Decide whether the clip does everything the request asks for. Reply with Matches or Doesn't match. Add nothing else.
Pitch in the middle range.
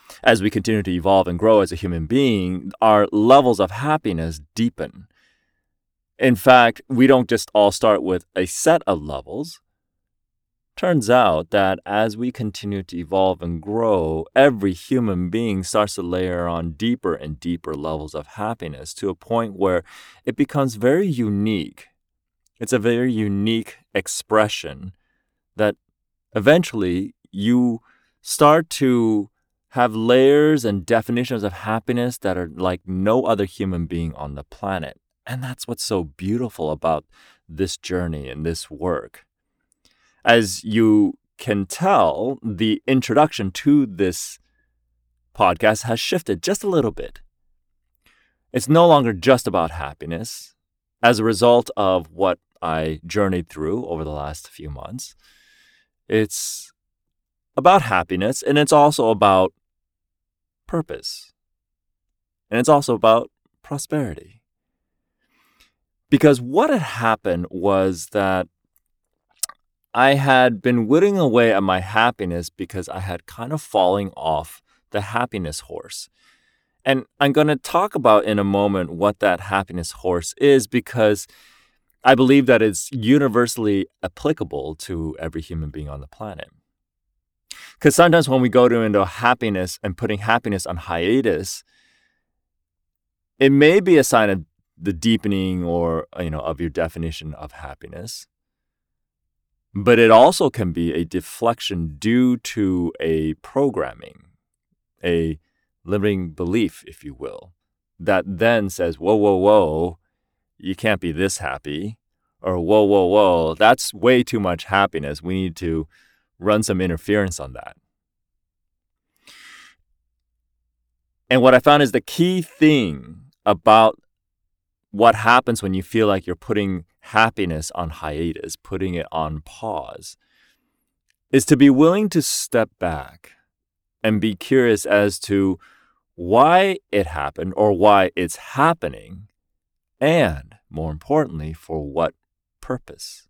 Doesn't match